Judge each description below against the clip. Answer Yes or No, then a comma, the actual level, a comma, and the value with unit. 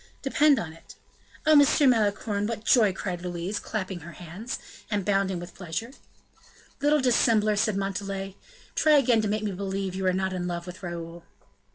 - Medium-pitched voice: No, high, 195 Hz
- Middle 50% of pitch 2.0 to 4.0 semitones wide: Yes, average, 3.7 semitones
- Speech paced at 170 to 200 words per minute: Yes, average, 175 wpm